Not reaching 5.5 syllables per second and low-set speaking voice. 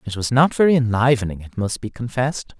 No: 6.1 syllables/s; low, 120 Hz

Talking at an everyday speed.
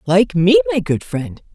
Yes: average, 195 wpm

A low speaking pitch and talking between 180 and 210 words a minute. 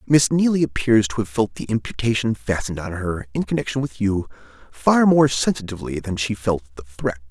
Yes: low, 110 Hz; average, 190 wpm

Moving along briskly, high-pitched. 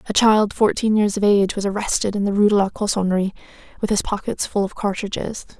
Yes: fast, 215 wpm; high, 205 Hz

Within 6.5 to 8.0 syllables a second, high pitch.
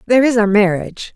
Yes: 7.4 syllables/s; high, 220 Hz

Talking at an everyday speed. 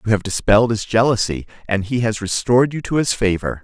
No: fast, 215 wpm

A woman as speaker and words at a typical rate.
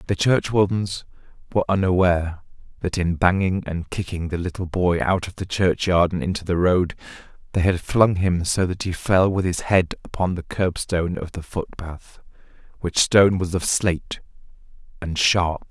No: male; average, 170 wpm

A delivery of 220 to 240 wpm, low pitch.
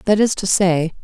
No: fast, 230 wpm; high, 190 Hz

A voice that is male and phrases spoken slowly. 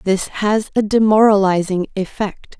No: female; slow, 115 wpm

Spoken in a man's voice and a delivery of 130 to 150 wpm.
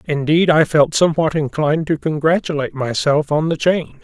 No: male; average, 165 wpm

